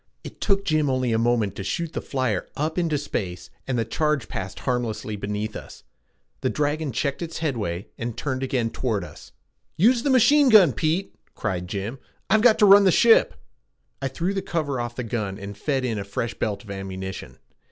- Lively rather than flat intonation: Yes, wide, 7.4 semitones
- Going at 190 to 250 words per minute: Yes, average, 195 wpm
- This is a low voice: Yes, low, 130 Hz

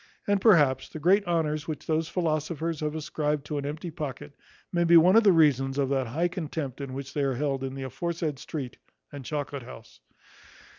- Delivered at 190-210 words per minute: Yes, average, 200 wpm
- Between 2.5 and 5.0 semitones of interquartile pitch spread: Yes, average, 3.3 semitones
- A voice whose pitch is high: No, medium, 150 Hz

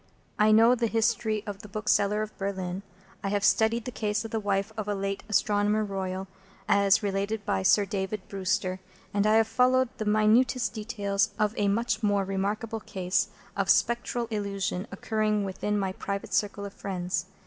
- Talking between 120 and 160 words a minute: No, average, 175 wpm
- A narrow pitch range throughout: Yes, narrow, 1.8 semitones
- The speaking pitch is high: Yes, high, 205 Hz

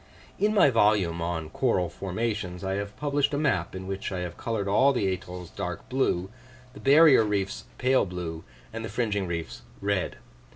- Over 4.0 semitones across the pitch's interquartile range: Yes, average, 5.0 semitones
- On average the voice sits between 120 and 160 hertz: No, low, 100 Hz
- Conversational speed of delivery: Yes, average, 175 wpm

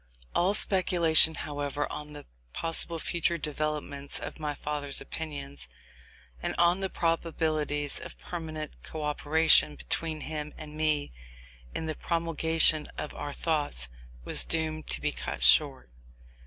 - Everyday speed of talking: No, slow, 130 wpm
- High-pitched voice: No, medium, 155 Hz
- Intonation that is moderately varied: No, narrow, 1.9 semitones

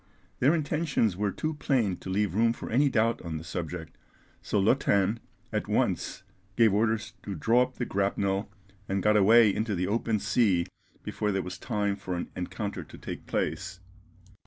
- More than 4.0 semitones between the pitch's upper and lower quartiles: No, average, 3.4 semitones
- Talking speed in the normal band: Yes, average, 175 wpm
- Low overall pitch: Yes, low, 105 Hz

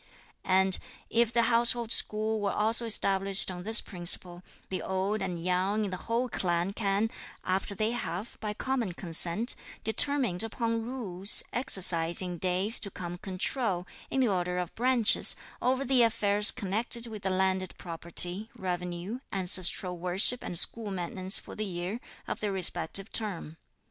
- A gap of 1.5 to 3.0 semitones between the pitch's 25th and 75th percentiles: No, average, 3.9 semitones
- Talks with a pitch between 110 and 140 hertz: No, high, 195 Hz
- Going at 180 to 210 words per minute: No, average, 155 wpm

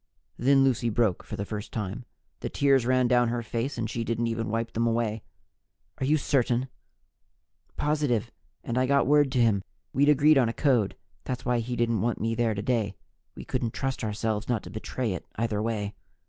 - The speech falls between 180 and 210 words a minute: Yes, average, 195 wpm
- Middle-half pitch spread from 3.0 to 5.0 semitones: No, narrow, 2.5 semitones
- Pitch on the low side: Yes, low, 120 Hz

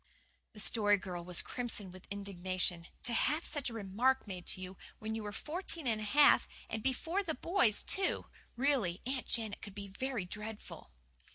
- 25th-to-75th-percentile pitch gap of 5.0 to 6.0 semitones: Yes, wide, 5.4 semitones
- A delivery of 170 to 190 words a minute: Yes, average, 180 wpm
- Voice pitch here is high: Yes, high, 215 Hz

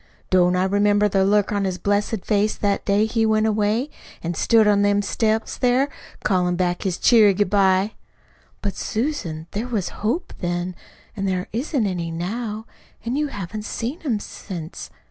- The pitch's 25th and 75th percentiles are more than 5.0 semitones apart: No, average, 3.0 semitones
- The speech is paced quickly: No, average, 170 wpm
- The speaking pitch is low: No, high, 205 Hz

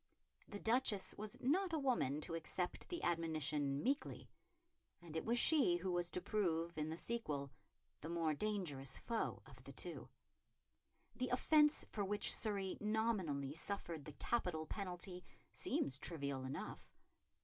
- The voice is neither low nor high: Yes, medium, 180 Hz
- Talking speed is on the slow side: No, average, 145 wpm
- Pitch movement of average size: No, wide, 6.0 semitones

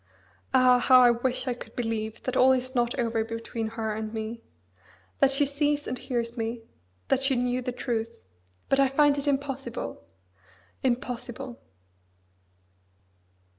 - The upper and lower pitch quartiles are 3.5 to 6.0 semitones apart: No, narrow, 2.6 semitones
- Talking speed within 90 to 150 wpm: Yes, average, 145 wpm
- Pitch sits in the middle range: No, high, 245 Hz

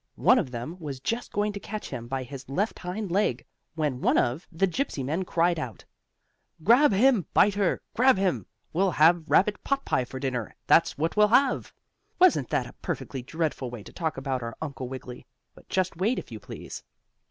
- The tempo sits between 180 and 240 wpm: Yes, average, 190 wpm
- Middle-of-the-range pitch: Yes, medium, 165 Hz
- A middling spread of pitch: No, wide, 7.7 semitones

